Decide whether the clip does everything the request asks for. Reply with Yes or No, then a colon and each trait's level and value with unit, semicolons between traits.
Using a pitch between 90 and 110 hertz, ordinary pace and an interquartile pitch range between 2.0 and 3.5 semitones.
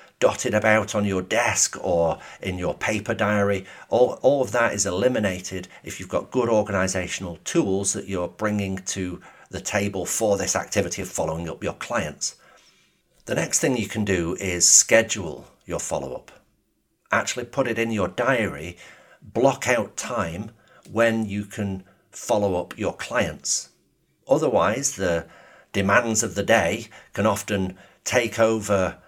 Yes: low, 100 Hz; average, 150 wpm; average, 2.8 semitones